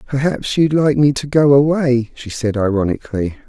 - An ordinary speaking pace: Yes, average, 170 wpm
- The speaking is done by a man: Yes, male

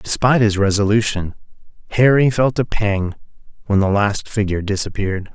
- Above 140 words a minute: No, slow, 135 wpm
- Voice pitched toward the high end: No, low, 105 Hz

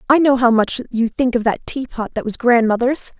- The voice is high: Yes, high, 240 Hz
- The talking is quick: Yes, fast, 225 wpm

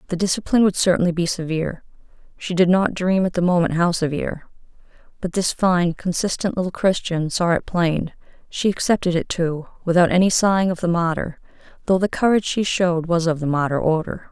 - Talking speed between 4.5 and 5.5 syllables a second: No, 5.8 syllables/s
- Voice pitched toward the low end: No, medium, 175 Hz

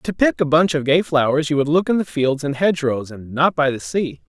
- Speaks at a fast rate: Yes, fast, 290 wpm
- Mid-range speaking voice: Yes, medium, 145 Hz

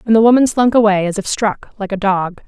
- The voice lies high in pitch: Yes, high, 210 Hz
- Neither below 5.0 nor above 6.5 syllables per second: Yes, 5.9 syllables/s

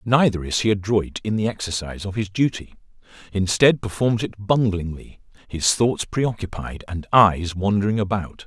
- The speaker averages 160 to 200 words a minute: No, average, 150 wpm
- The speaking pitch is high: No, low, 100 Hz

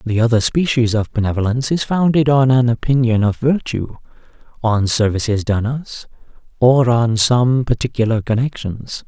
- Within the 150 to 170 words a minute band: No, average, 140 wpm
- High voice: No, low, 120 Hz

